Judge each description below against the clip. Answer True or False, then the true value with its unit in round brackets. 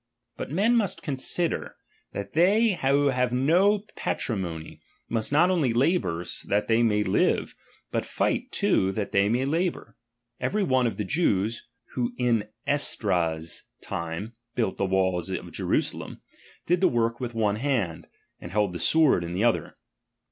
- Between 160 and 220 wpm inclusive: True (175 wpm)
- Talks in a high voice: False (115 Hz)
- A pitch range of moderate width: False (6.8 semitones)